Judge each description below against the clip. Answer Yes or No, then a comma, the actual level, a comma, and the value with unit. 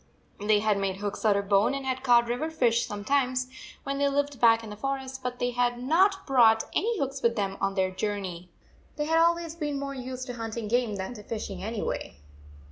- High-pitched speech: Yes, high, 245 Hz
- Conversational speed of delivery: No, fast, 220 wpm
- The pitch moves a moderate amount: Yes, average, 4.7 semitones